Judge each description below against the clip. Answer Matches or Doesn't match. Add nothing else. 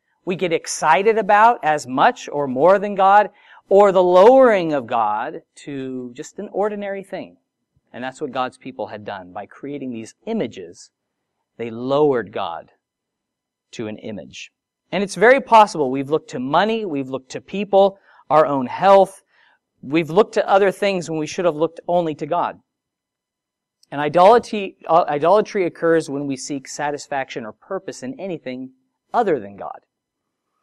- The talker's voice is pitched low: Doesn't match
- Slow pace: Doesn't match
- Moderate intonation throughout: Doesn't match